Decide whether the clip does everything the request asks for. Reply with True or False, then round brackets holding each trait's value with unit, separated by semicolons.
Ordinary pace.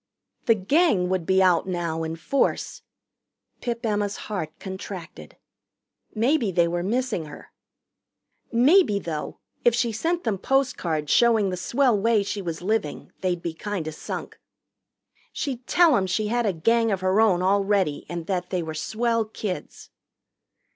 True (155 wpm)